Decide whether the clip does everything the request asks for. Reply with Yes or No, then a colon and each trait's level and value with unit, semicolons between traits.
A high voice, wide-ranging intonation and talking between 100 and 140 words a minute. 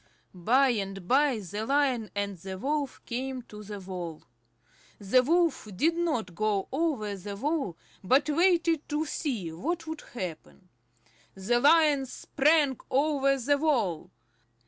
Yes: very high, 255 Hz; wide, 6.9 semitones; slow, 135 wpm